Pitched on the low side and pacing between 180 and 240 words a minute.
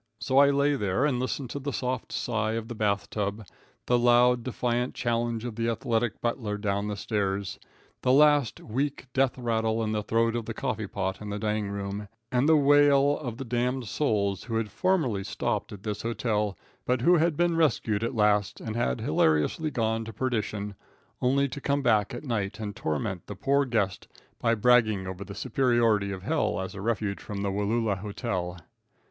Yes: low, 115 Hz; average, 190 wpm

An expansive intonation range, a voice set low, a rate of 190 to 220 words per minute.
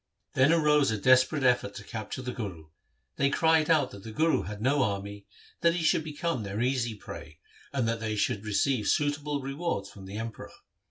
Yes: wide, 5.8 semitones; low, 125 Hz; average, 195 wpm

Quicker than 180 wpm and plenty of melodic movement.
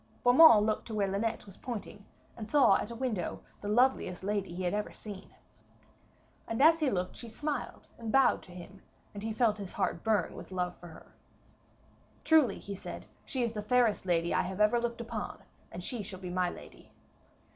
No: average, 200 wpm; average, 4.1 semitones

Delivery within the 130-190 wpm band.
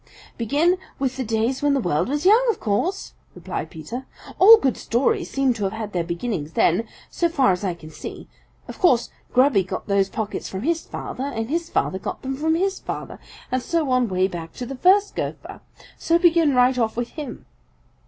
No: average, 200 wpm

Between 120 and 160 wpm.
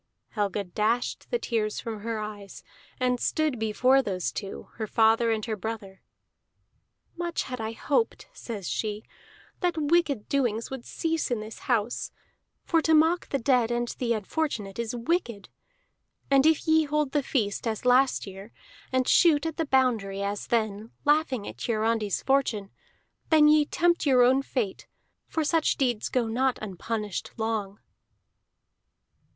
Yes: average, 150 wpm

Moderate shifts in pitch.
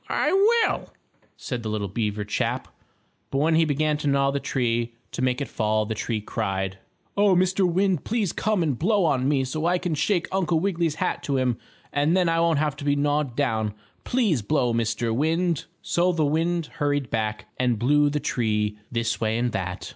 No: wide, 6.4 semitones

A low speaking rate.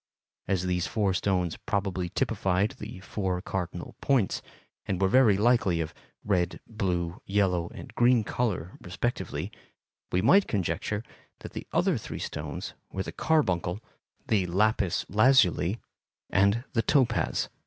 Yes: slow, 130 wpm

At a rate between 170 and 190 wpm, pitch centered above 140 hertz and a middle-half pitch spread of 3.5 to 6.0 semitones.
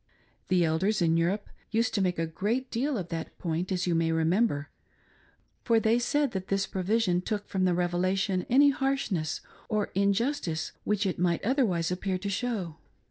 Yes: average, 180 wpm; high, 190 Hz; average, 4.3 semitones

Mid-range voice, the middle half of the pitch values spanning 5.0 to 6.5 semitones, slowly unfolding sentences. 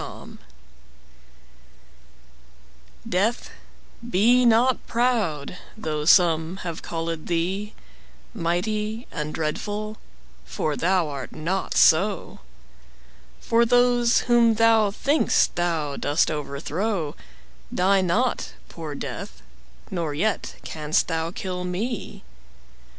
Yes: medium, 180 Hz; wide, 5.5 semitones; slow, 95 wpm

